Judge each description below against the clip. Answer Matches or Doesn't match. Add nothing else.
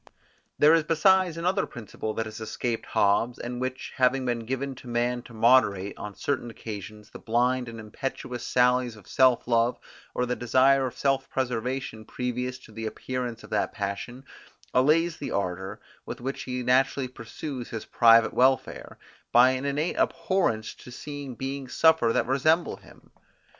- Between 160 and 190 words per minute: Matches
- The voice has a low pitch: Matches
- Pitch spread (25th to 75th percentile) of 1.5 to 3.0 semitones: Matches